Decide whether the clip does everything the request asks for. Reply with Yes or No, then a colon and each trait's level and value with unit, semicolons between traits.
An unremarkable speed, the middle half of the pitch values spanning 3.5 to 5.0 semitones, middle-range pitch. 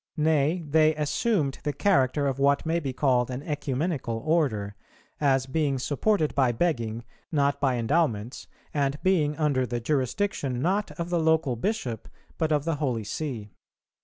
Yes: average, 155 wpm; average, 3.8 semitones; medium, 145 Hz